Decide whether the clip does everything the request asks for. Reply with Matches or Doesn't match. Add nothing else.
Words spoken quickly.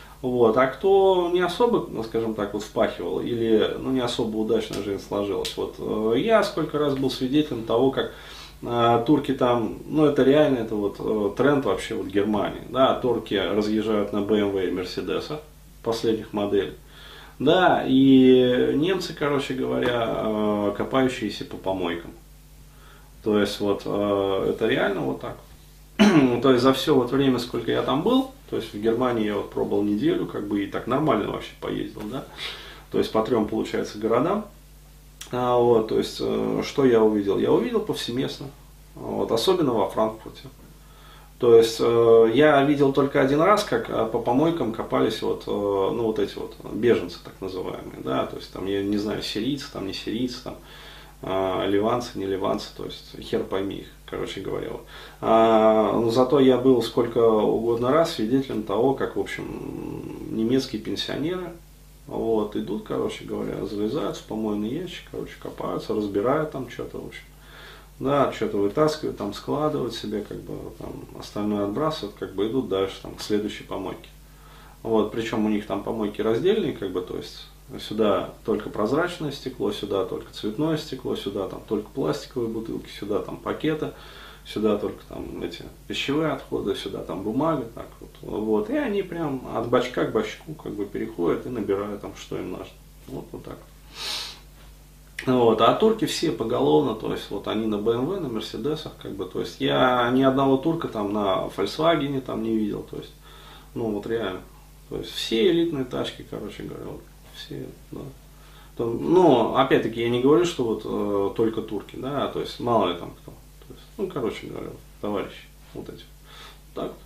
Matches